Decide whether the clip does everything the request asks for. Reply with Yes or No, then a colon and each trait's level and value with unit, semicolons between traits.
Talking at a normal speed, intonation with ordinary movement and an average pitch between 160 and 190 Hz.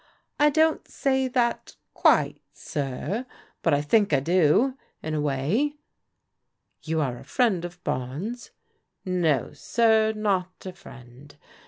No: average, 145 wpm; wide, 8.2 semitones; medium, 185 Hz